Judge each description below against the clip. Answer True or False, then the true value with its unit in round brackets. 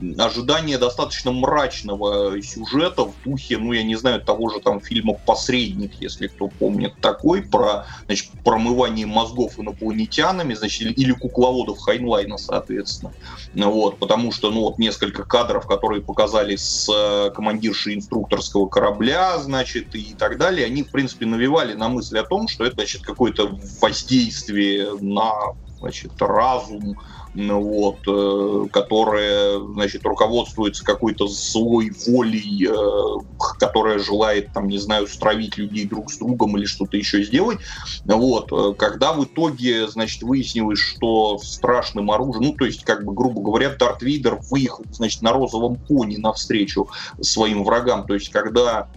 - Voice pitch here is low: True (110 Hz)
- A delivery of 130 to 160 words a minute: True (135 wpm)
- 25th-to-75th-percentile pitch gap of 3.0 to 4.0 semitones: True (3.3 semitones)